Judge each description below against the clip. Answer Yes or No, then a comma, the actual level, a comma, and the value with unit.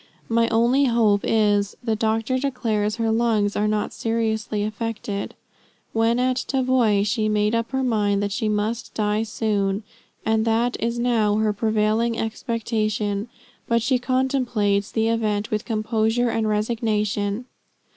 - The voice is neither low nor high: No, high, 220 Hz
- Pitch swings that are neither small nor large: No, narrow, 1.8 semitones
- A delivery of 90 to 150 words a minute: Yes, average, 140 wpm